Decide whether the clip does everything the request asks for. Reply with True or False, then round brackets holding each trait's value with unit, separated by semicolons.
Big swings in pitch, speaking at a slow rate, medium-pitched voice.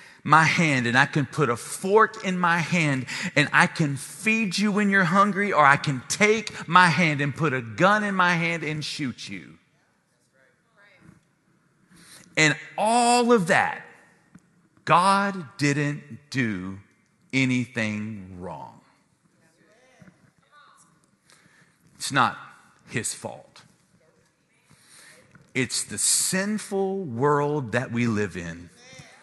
True (6.3 semitones; 115 wpm; 160 Hz)